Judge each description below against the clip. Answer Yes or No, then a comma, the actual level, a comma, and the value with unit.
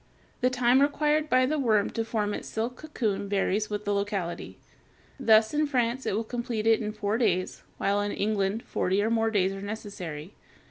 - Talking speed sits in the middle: Yes, average, 190 wpm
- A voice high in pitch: Yes, high, 220 Hz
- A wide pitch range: No, average, 3.3 semitones